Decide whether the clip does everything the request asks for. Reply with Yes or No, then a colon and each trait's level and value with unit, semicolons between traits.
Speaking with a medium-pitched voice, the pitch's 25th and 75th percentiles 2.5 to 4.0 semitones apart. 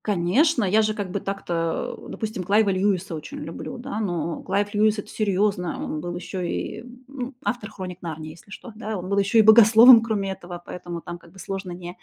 No: high, 195 Hz; average, 3.5 semitones